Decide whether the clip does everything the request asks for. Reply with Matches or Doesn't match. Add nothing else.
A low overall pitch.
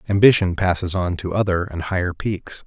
Matches